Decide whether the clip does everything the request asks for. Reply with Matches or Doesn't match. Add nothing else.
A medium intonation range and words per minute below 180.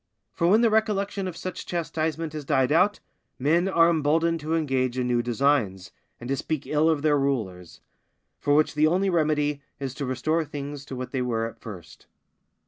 Doesn't match